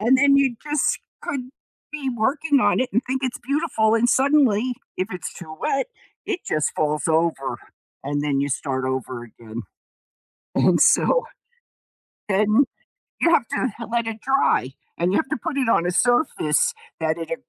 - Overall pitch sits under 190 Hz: No, high, 225 Hz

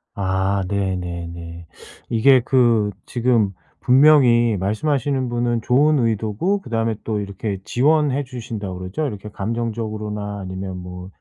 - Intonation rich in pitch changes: No, average, 4.3 semitones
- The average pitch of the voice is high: No, low, 110 Hz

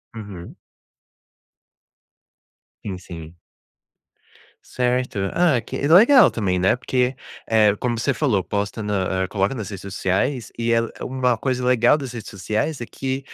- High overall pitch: No, low, 115 Hz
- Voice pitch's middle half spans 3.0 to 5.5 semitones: Yes, average, 4.5 semitones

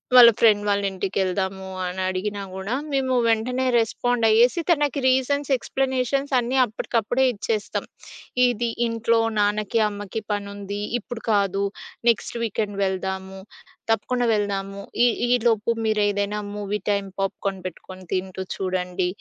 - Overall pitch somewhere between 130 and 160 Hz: No, high, 205 Hz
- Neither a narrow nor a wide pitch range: Yes, average, 3.3 semitones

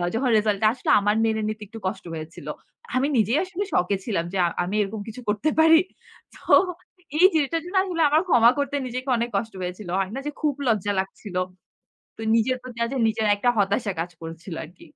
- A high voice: Yes, high, 220 Hz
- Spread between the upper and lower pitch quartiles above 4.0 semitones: Yes, average, 4.8 semitones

